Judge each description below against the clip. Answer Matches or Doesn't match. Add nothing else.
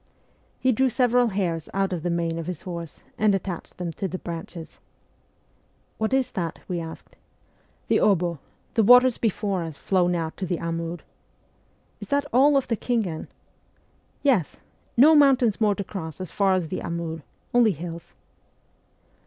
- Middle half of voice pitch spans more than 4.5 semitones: Matches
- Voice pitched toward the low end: Doesn't match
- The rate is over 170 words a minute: Matches